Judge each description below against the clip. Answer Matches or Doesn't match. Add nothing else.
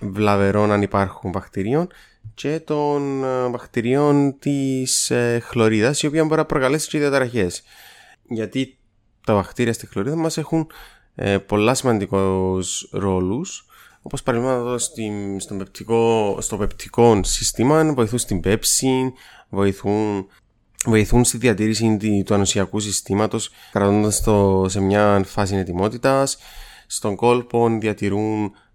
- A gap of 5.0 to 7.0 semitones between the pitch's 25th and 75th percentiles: Doesn't match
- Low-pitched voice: Matches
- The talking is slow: Matches